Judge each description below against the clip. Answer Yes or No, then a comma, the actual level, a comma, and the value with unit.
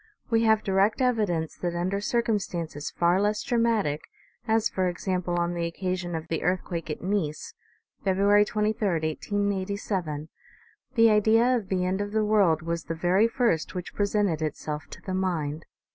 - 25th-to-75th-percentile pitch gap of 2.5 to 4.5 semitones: Yes, average, 3.8 semitones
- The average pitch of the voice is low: No, medium, 185 Hz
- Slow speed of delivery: No, average, 160 wpm